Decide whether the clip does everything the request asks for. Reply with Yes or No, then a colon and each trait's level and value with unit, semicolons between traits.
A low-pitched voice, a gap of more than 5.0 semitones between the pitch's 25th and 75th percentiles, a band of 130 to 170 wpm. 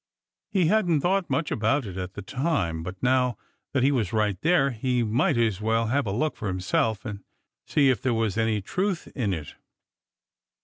No: low, 115 Hz; wide, 5.4 semitones; average, 190 wpm